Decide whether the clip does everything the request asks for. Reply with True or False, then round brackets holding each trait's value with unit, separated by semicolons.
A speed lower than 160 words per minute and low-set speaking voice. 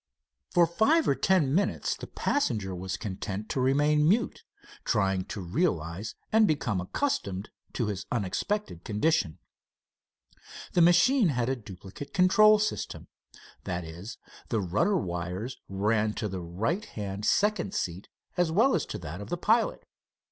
True (145 wpm; 115 Hz)